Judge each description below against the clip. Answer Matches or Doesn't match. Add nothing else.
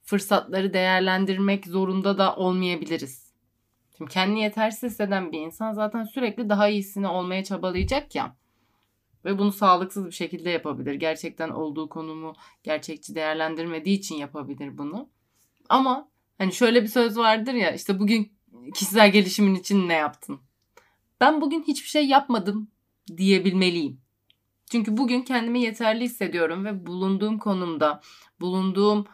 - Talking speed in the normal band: Matches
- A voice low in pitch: Doesn't match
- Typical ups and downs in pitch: Matches